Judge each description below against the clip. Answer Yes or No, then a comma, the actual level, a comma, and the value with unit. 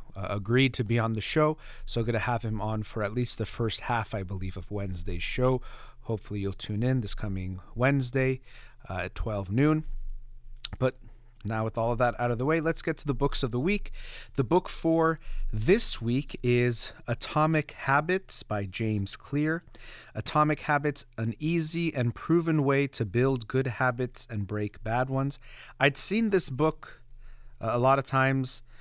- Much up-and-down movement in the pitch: No, average, 3.8 semitones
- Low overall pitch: Yes, low, 125 Hz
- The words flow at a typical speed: Yes, average, 180 wpm